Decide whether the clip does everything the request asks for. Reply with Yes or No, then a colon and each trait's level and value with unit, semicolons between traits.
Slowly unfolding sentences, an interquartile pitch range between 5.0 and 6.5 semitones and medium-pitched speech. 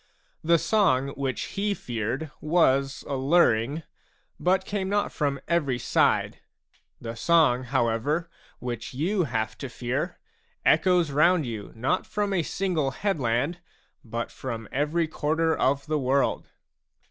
Yes: slow, 125 wpm; average, 5.3 semitones; medium, 145 Hz